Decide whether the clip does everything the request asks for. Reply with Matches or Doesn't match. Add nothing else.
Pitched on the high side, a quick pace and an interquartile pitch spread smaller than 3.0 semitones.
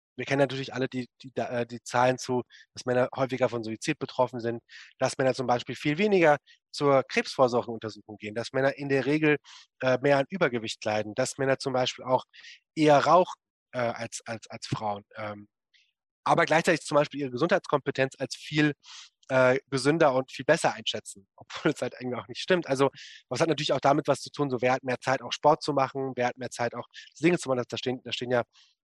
Doesn't match